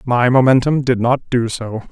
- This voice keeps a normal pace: Yes, average, 190 wpm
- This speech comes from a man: Yes, male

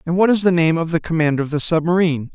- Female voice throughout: No, male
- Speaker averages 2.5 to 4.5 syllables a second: No, 7.2 syllables/s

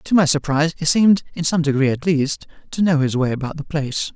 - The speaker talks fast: Yes, fast, 245 wpm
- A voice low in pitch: No, medium, 155 Hz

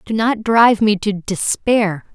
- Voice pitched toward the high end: Yes, high, 210 Hz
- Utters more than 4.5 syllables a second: No, 4.0 syllables/s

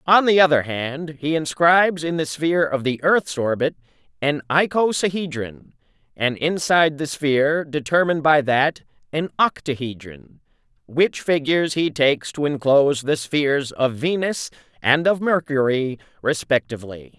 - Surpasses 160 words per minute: No, slow, 135 wpm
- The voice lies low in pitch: No, medium, 145 Hz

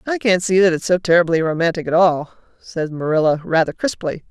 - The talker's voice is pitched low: No, medium, 170 Hz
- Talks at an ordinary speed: Yes, average, 195 wpm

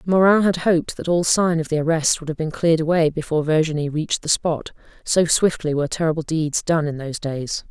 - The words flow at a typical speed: No, fast, 210 wpm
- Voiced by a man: No, female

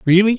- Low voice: No, high, 200 Hz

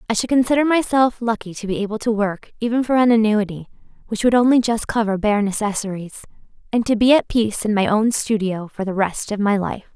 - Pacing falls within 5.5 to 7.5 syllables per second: Yes, 5.9 syllables/s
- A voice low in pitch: No, high, 220 Hz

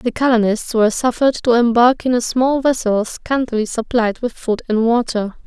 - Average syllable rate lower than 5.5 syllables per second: Yes, 5.1 syllables/s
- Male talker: No, female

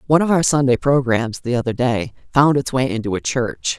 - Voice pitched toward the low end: Yes, low, 130 Hz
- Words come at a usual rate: No, fast, 220 wpm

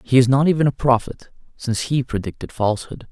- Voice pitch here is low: Yes, low, 125 Hz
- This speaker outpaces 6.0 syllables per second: Yes, 6.2 syllables/s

